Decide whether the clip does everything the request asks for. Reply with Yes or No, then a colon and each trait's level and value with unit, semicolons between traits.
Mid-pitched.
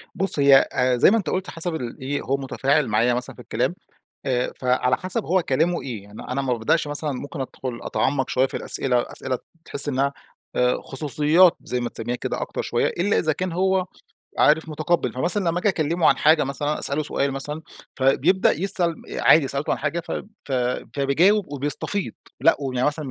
Yes: medium, 145 Hz